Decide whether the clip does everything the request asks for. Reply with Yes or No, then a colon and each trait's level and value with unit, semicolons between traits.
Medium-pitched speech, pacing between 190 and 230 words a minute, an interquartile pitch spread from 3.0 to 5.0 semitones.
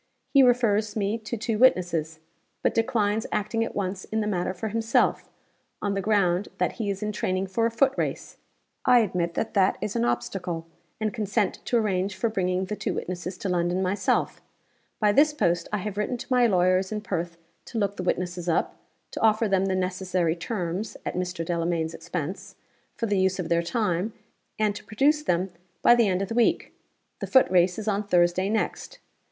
No: high, 195 Hz; average, 195 wpm; average, 3.4 semitones